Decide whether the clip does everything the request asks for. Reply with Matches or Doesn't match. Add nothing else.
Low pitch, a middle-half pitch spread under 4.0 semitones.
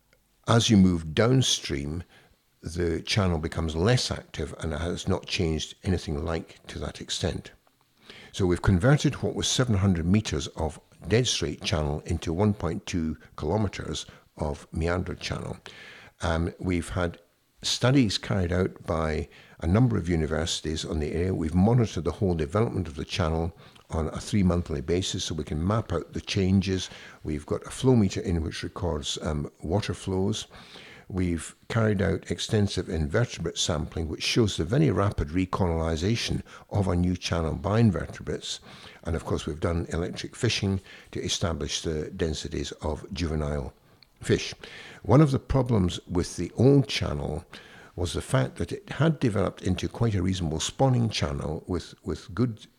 Doesn't match